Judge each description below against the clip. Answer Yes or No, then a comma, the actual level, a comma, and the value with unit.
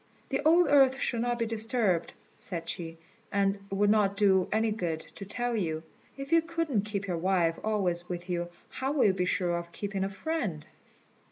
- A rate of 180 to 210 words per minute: Yes, average, 195 wpm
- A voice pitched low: No, high, 200 Hz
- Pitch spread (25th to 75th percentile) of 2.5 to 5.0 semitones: No, wide, 5.4 semitones